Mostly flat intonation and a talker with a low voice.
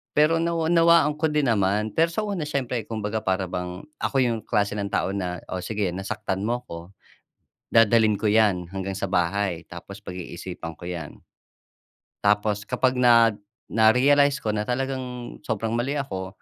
No: average, 4.9 semitones; low, 110 Hz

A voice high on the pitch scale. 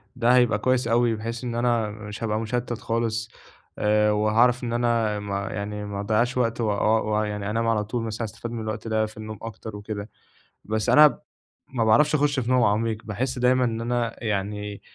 No: low, 110 Hz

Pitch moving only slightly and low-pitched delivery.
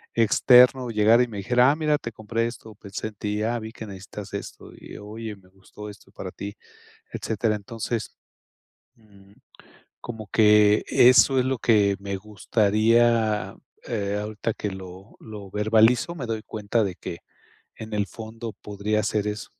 Yes: narrow, 2.0 semitones; low, 110 Hz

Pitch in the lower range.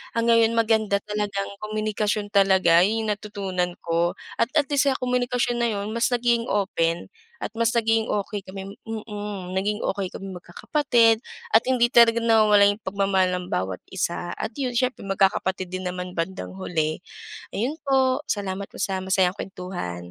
No: high, 205 Hz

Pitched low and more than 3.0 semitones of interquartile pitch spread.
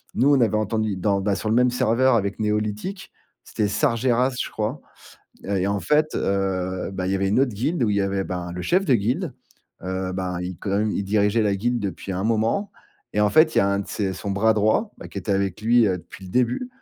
Yes: low, 105 Hz; average, 3.5 semitones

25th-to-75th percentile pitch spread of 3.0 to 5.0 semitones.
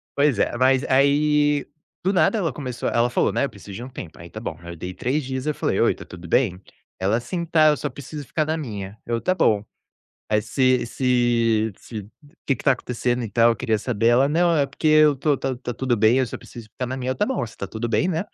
Yes: average, 4.5 semitones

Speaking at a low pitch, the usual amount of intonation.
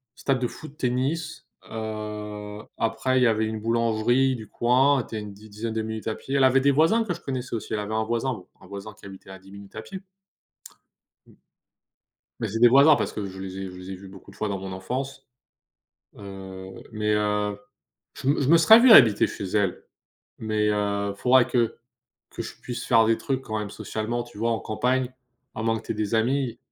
Yes: low, 110 Hz; average, 3.6 semitones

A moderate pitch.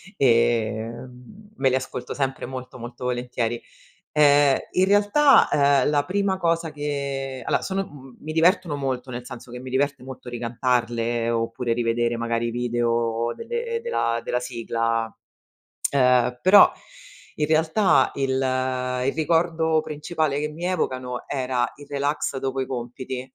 No: low, 130 Hz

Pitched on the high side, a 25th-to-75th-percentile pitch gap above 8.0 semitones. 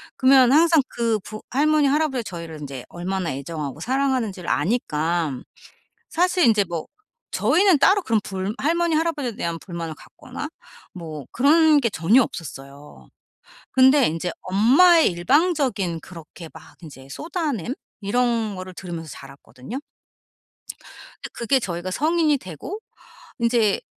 Yes: high, 220 Hz; wide, 9.0 semitones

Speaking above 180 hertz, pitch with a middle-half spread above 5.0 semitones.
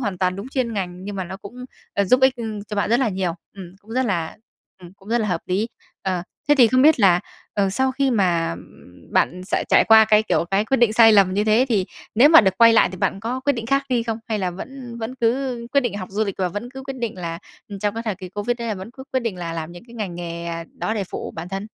No: high, 210 Hz; average, 4.3 semitones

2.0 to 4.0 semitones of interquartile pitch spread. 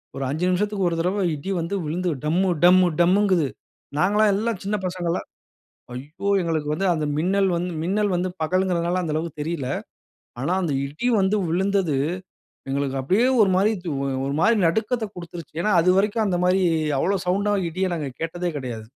Yes: average, 3.3 semitones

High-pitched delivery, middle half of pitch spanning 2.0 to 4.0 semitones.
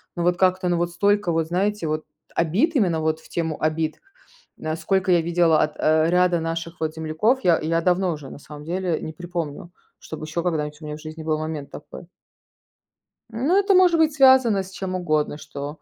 No: medium, 170 Hz; average, 3.0 semitones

